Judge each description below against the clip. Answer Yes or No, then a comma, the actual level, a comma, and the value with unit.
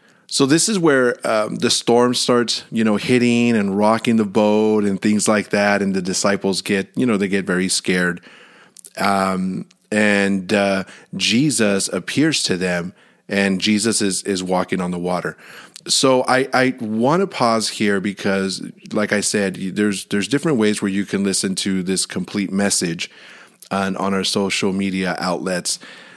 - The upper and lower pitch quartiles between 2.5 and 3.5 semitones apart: Yes, average, 2.8 semitones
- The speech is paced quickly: No, average, 165 wpm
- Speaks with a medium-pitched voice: No, low, 100 Hz